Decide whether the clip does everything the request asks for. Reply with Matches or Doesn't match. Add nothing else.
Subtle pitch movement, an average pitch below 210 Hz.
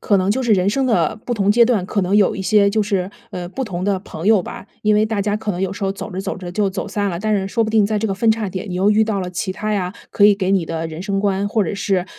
Matches